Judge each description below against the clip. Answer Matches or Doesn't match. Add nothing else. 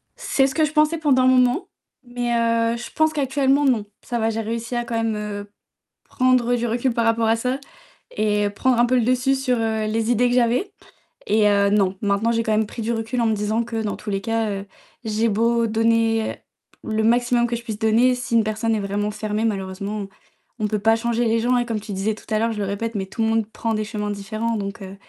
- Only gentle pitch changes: Matches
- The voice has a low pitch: Doesn't match